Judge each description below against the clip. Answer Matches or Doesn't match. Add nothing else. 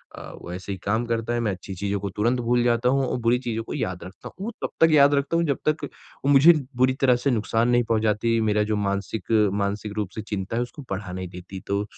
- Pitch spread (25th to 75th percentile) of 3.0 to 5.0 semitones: Matches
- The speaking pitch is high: Doesn't match